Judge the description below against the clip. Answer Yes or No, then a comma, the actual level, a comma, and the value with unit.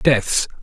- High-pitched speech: No, low, 125 Hz